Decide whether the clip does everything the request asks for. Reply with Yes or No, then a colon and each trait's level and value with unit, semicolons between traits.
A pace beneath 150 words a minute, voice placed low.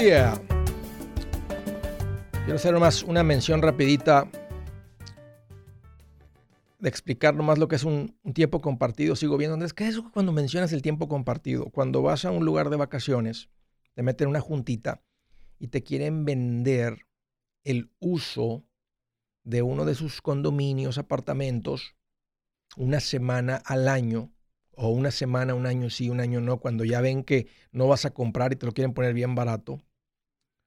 No: average, 155 wpm; low, 125 Hz